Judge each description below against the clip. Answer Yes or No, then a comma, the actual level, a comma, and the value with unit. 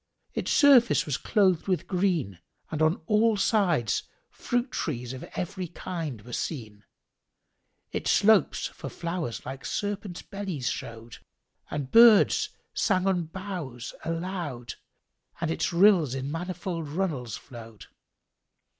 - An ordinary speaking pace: No, slow, 120 wpm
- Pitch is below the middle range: No, medium, 170 Hz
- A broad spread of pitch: Yes, wide, 6.6 semitones